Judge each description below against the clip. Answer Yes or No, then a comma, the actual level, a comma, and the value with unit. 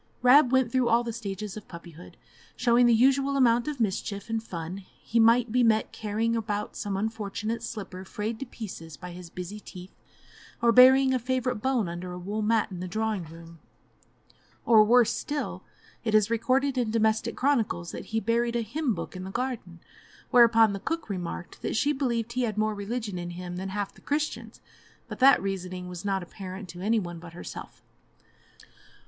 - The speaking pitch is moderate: No, high, 220 Hz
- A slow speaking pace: No, average, 190 wpm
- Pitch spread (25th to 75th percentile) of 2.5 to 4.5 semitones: Yes, average, 4.2 semitones